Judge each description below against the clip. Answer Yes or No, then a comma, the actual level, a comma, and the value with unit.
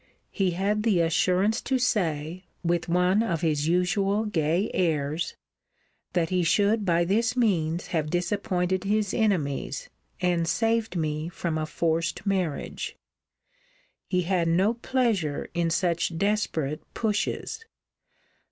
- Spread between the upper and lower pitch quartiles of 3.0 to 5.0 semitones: Yes, average, 3.8 semitones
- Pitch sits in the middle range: Yes, medium, 180 Hz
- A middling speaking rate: No, slow, 125 wpm